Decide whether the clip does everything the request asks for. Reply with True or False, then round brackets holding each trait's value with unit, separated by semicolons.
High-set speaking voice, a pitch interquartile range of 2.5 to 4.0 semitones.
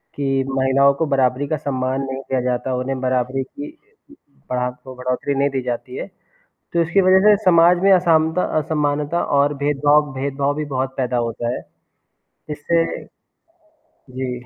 False (135 Hz; 2.8 semitones)